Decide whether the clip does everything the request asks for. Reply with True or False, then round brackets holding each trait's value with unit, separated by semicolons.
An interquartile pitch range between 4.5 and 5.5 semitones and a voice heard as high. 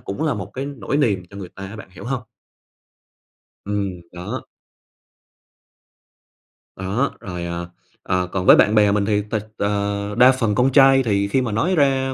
False (4.8 semitones; 105 Hz)